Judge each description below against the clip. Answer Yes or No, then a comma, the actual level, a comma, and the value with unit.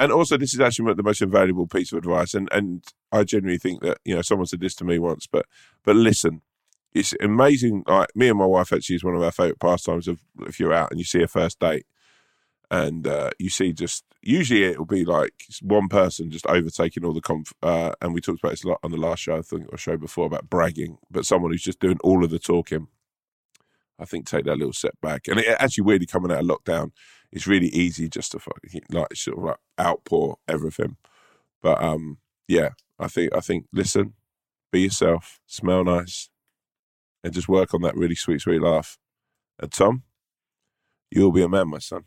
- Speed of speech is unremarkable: No, fast, 220 wpm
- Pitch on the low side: Yes, very low, 90 Hz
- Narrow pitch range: No, average, 3.2 semitones